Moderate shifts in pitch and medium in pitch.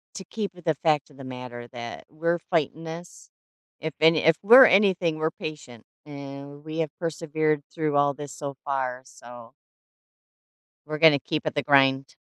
Yes: average, 3.0 semitones; medium, 150 Hz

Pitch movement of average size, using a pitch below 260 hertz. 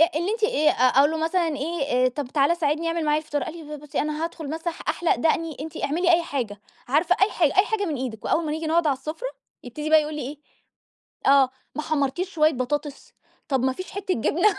No: average, 3.1 semitones; very high, 310 Hz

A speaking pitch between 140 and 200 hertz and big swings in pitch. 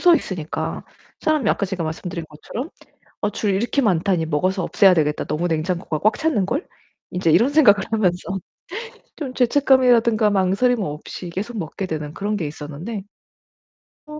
Yes: high, 195 Hz; wide, 5.9 semitones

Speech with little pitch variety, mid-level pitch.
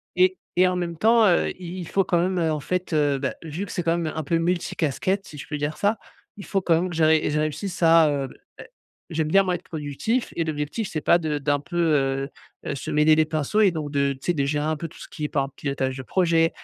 No: average, 3.4 semitones; medium, 160 Hz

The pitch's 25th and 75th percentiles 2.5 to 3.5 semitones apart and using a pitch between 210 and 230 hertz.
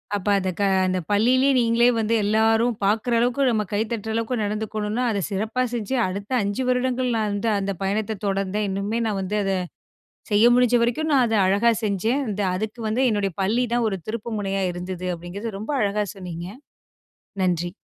Yes: average, 3.0 semitones; high, 215 Hz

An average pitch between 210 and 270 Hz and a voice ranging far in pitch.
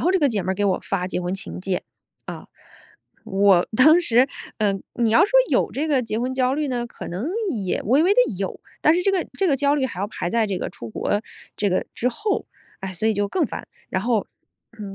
Yes: high, 225 Hz; wide, 6.5 semitones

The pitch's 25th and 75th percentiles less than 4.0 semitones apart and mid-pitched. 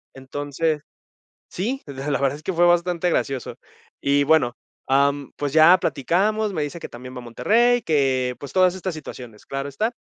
No: average, 4.6 semitones; medium, 145 Hz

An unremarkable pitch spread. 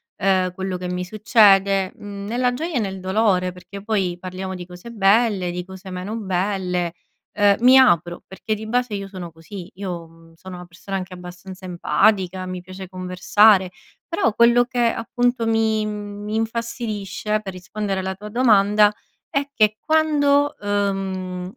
Yes: average, 3.1 semitones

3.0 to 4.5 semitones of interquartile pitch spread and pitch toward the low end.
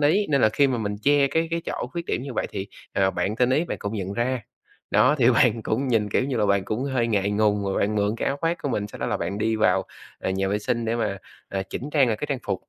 No: average, 5.0 semitones; low, 115 Hz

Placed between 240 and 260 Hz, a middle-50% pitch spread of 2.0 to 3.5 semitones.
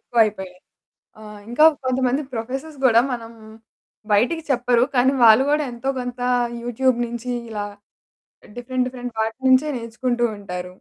Yes: high, 245 Hz; narrow, 2.4 semitones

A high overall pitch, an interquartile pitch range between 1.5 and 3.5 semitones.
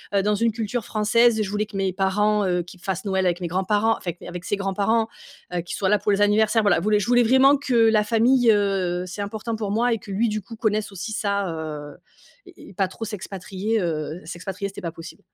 Yes: high, 205 Hz; average, 2.7 semitones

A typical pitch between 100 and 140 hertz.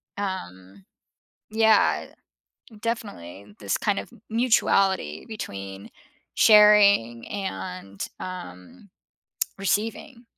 No: high, 190 Hz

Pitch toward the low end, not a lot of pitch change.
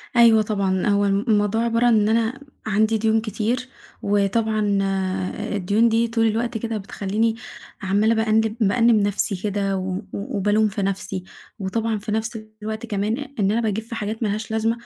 No: high, 215 Hz; narrow, 2.0 semitones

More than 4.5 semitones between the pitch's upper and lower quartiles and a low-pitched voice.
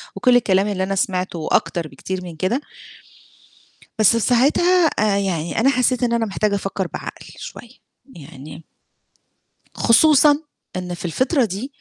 No: wide, 5.6 semitones; high, 200 Hz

